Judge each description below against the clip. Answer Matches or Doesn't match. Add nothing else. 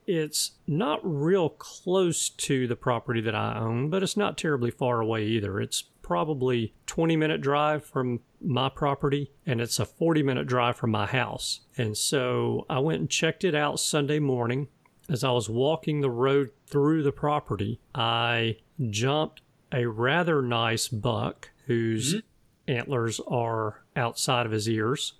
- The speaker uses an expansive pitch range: Doesn't match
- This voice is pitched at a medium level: Doesn't match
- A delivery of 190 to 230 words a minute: Doesn't match